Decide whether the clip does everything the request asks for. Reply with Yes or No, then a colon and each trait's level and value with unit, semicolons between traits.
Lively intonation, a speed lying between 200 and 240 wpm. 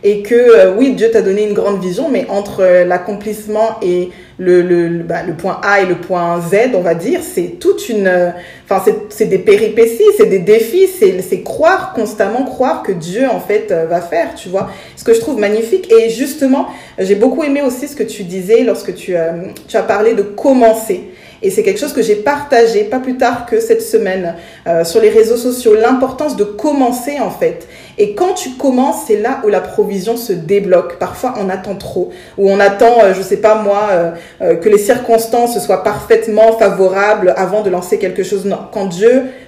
Yes: wide, 6.7 semitones; average, 215 wpm